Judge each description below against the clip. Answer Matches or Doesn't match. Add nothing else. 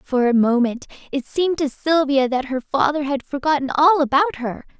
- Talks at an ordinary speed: Matches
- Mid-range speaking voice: Doesn't match